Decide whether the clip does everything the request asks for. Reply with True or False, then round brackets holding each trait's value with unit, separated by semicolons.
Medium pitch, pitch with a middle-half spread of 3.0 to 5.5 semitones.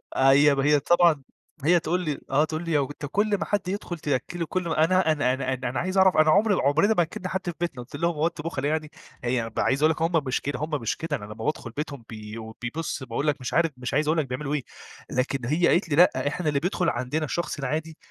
True (150 Hz; 4.0 semitones)